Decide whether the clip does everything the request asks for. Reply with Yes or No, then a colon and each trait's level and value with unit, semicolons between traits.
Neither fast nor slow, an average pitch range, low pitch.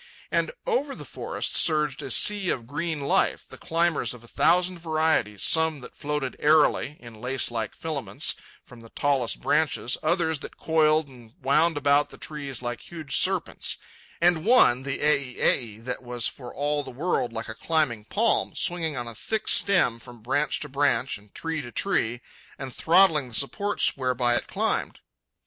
No: average, 170 wpm; average, 4.7 semitones; medium, 145 Hz